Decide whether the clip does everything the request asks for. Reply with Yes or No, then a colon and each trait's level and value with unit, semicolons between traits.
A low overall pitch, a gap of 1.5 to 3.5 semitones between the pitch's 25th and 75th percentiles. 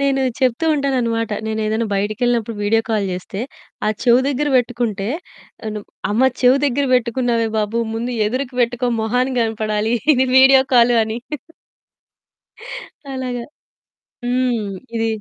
No: high, 235 Hz; narrow, 2.5 semitones